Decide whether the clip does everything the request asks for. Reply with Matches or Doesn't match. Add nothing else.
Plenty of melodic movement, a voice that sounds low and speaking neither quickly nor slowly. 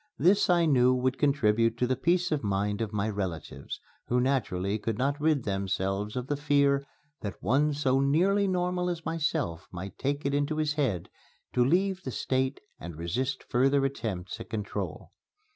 Matches